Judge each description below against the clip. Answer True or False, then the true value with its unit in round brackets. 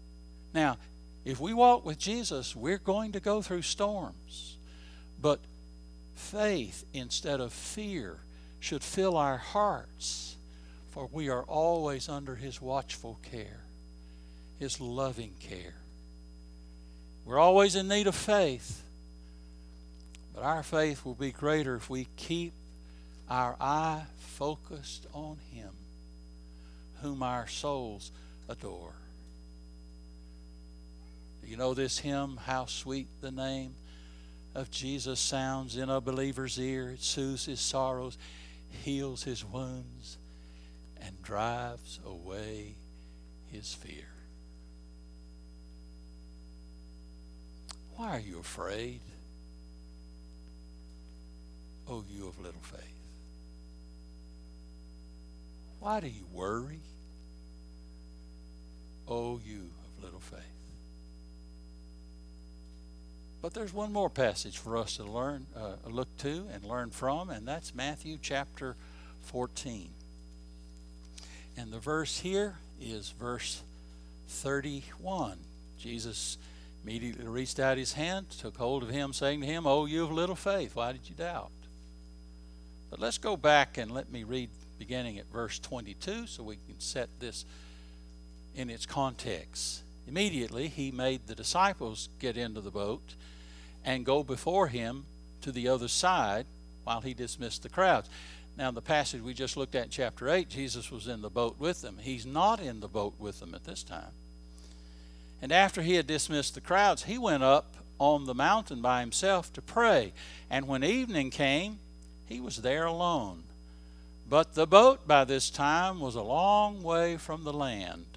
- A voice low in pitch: True (100 Hz)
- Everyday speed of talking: False (130 wpm)